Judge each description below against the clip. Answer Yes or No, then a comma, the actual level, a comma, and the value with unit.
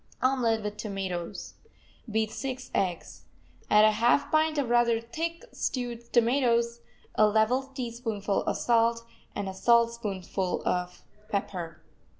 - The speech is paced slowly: Yes, slow, 125 wpm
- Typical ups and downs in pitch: Yes, average, 3.0 semitones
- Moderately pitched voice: No, high, 230 Hz